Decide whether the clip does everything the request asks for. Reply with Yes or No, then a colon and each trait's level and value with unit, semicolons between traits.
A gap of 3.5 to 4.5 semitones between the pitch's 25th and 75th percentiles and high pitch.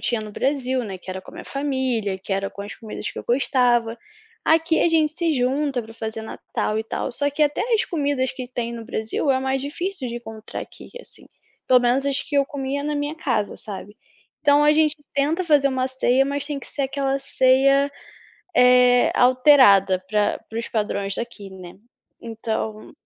Yes: average, 4.2 semitones; very high, 260 Hz